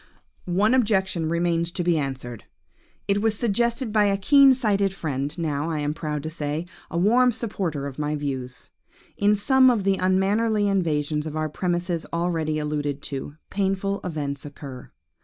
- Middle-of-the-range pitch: Yes, medium, 170 Hz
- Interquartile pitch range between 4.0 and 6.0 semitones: Yes, average, 5.2 semitones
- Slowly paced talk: No, average, 160 wpm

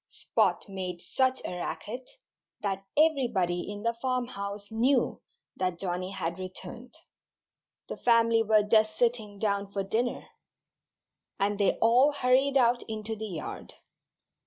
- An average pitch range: Yes, average, 3.8 semitones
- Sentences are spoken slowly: Yes, slow, 130 wpm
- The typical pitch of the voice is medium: No, high, 215 Hz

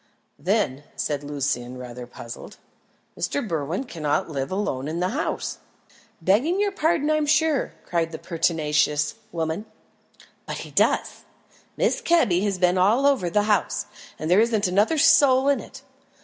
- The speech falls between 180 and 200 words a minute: No, average, 150 wpm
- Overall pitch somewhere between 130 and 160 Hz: No, medium, 185 Hz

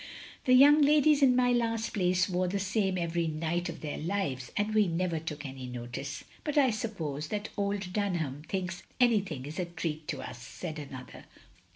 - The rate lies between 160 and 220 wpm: Yes, average, 190 wpm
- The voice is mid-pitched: Yes, medium, 180 Hz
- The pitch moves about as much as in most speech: No, wide, 5.7 semitones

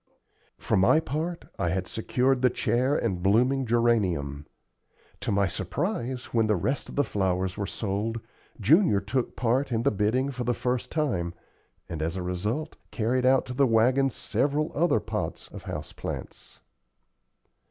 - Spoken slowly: No, average, 160 wpm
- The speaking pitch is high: No, low, 120 Hz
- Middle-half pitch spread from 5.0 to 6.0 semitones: Yes, wide, 5.4 semitones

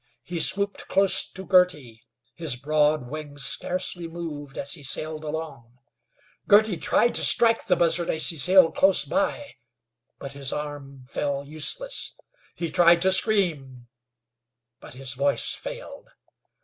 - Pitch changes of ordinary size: Yes, average, 5.0 semitones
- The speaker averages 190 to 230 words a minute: No, slow, 135 wpm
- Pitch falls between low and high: Yes, medium, 155 Hz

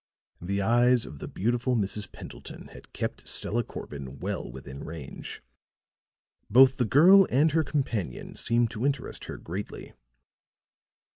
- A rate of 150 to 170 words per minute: No, slow, 135 wpm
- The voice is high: No, low, 115 Hz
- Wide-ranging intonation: Yes, wide, 6.5 semitones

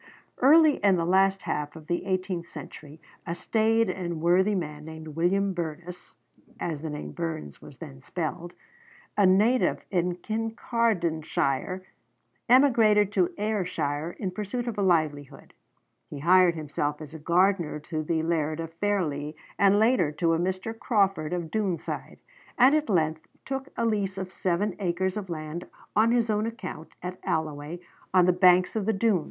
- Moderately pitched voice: Yes, medium, 180 Hz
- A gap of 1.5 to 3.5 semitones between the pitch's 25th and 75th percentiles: No, average, 4.4 semitones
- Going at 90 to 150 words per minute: No, average, 160 wpm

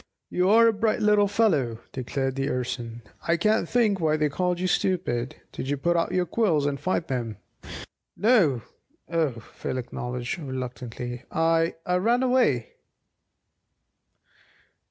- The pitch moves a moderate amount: No, wide, 7.1 semitones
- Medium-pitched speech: Yes, medium, 160 Hz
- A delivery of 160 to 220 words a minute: No, slow, 135 wpm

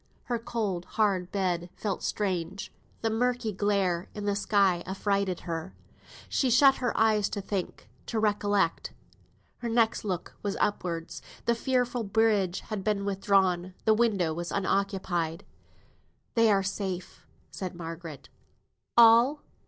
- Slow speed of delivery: Yes, slow, 130 wpm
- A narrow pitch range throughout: No, average, 3.4 semitones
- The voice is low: No, high, 200 Hz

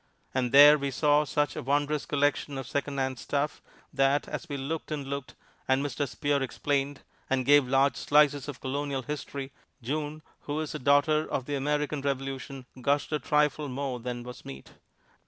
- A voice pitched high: No, medium, 140 Hz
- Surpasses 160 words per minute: Yes, average, 175 wpm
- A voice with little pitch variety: Yes, narrow, 1.6 semitones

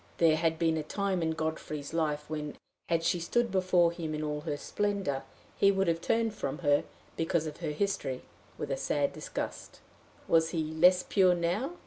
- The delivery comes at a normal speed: Yes, average, 185 wpm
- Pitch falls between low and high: Yes, medium, 165 Hz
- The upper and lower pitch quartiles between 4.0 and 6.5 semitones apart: No, average, 3.1 semitones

